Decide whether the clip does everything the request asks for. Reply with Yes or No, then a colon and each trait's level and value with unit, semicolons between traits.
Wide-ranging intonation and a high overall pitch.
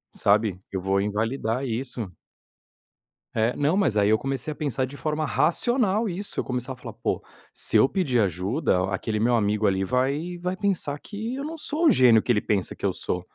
No: wide, 8.0 semitones; low, 130 Hz